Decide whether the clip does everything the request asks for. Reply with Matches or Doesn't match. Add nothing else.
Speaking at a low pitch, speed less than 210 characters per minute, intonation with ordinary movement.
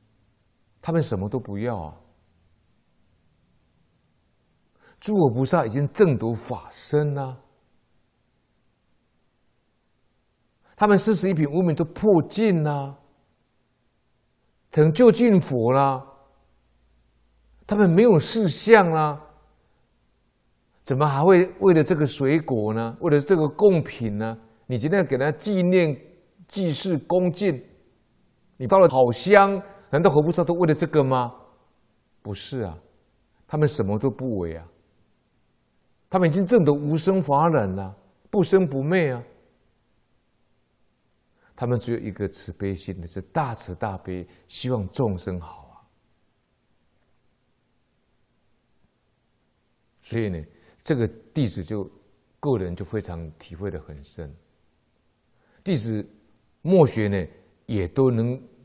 Doesn't match